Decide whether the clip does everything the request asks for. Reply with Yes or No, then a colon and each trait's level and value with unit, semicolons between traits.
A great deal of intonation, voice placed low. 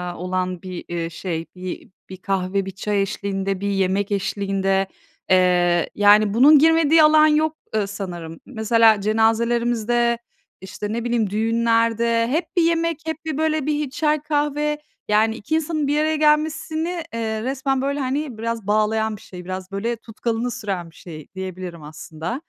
No: wide, 7.0 semitones; high, 225 Hz